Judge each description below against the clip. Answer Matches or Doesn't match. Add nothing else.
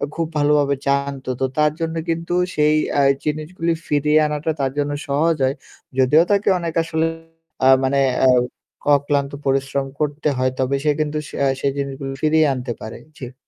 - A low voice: Doesn't match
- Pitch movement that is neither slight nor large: Doesn't match